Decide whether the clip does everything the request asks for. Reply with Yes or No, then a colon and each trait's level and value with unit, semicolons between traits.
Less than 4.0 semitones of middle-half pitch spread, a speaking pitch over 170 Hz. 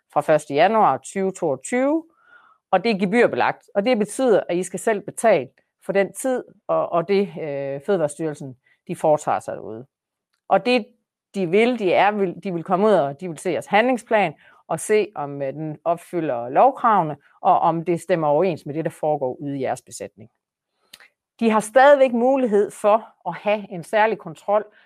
No: average, 5.2 semitones; high, 190 Hz